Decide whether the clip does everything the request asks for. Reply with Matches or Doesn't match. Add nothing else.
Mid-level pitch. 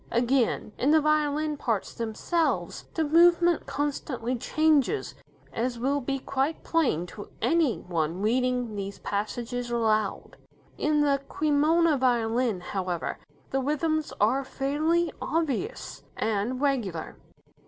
Doesn't match